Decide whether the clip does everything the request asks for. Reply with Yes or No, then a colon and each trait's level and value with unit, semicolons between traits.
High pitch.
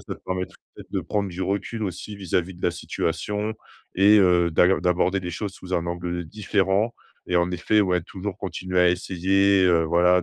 No: very low, 90 Hz